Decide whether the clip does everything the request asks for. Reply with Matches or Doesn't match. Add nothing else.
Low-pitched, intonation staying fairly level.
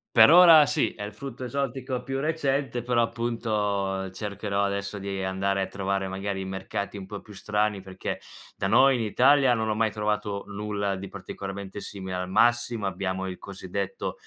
Doesn't match